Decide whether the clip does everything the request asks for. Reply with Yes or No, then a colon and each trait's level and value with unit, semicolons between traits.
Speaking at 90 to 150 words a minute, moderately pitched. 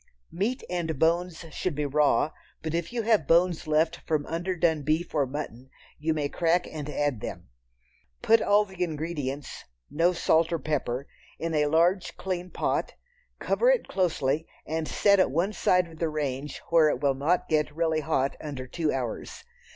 No: average, 175 wpm; medium, 160 Hz